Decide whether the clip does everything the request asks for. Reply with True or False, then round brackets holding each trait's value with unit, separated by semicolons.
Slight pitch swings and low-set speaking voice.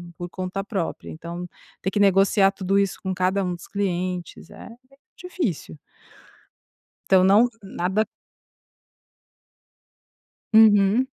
False (1.9 semitones; 195 Hz)